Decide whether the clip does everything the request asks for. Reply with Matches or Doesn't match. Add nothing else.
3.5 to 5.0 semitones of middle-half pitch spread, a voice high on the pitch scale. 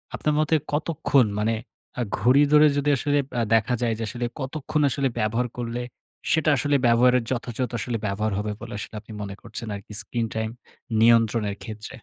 Doesn't match